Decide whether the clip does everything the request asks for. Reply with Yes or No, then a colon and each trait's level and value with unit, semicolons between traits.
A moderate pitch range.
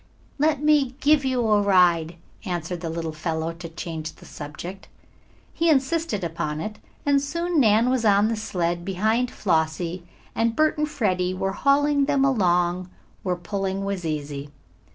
No: wide, 7.4 semitones